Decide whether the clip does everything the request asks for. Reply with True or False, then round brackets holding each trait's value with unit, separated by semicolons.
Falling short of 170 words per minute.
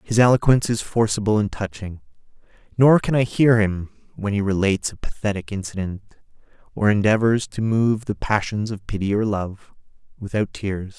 True (160 wpm)